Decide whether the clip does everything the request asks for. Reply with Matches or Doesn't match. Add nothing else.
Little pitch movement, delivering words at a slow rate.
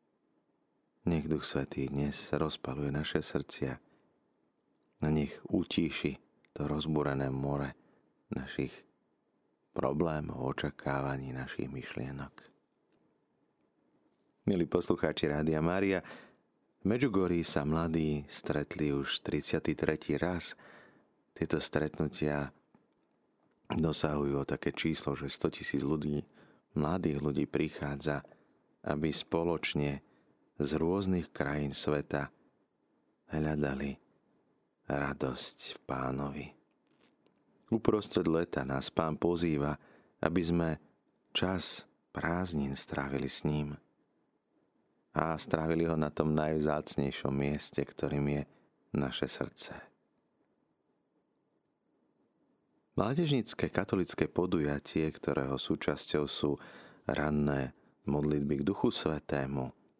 Matches